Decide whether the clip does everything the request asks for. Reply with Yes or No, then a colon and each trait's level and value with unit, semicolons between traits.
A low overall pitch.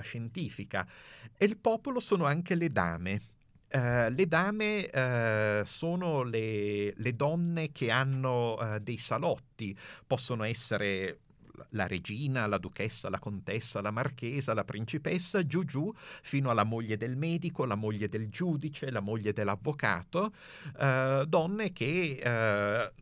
Yes: low, 125 Hz